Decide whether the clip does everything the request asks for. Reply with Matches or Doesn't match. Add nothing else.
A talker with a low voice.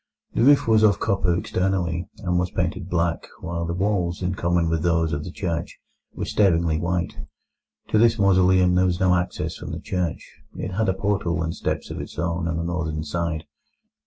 Matches